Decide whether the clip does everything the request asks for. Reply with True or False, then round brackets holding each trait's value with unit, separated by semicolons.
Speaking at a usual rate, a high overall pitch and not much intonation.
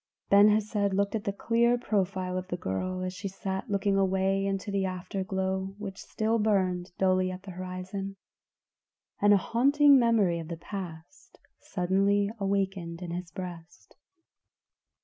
True (150 wpm; 195 Hz; 1.8 semitones)